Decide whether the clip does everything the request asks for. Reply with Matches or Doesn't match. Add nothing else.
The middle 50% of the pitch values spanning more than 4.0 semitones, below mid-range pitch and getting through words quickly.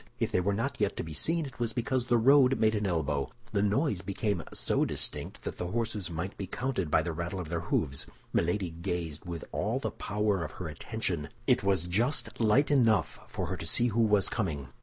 Matches